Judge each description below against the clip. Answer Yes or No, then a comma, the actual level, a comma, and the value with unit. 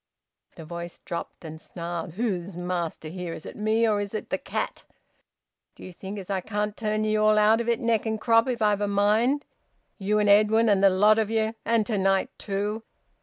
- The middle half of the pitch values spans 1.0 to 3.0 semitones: Yes, narrow, 2.6 semitones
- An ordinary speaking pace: No, fast, 210 wpm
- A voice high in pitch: Yes, high, 210 Hz